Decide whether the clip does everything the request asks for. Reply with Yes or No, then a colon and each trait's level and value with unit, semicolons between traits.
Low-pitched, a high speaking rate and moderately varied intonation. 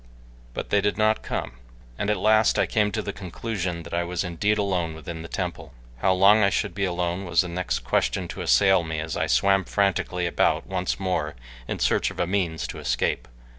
Yes: very low, 90 Hz; fast, 210 wpm; average, 3.0 semitones